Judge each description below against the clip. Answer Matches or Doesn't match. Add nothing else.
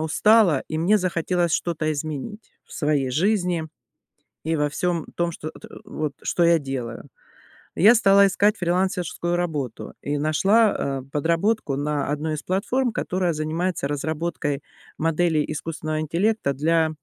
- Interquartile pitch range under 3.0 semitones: Doesn't match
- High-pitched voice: Doesn't match